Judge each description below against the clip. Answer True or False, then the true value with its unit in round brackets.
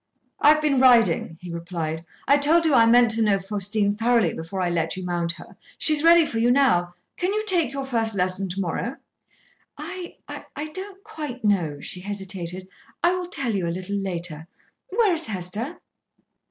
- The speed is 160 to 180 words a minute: False (190 wpm)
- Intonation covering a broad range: True (8.5 semitones)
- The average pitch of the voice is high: True (220 Hz)